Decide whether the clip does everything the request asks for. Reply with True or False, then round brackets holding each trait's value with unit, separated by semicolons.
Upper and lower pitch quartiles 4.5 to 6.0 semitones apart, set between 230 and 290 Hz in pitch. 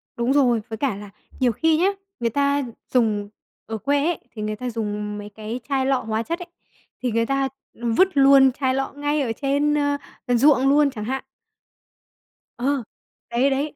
False (3.9 semitones; 265 Hz)